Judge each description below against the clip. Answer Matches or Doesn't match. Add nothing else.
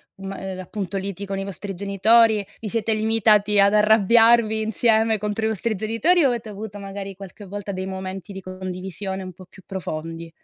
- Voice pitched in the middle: Doesn't match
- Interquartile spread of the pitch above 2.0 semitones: Matches